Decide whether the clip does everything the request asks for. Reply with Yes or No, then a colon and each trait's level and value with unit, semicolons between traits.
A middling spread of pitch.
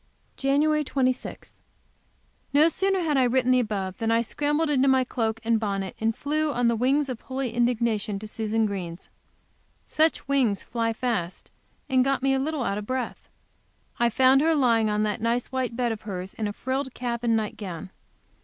Yes: average, 3.6 semitones